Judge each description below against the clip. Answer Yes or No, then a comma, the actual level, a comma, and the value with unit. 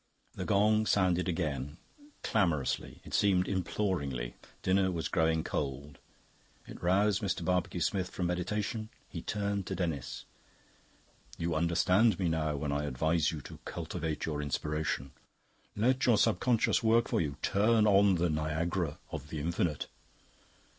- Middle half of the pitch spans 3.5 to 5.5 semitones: Yes, average, 4.7 semitones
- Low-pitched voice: Yes, very low, 85 Hz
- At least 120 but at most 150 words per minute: Yes, average, 140 wpm